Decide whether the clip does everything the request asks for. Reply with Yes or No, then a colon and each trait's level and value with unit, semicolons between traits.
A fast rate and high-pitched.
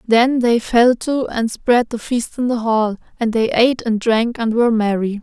Yes: fast, 220 wpm; high, 230 Hz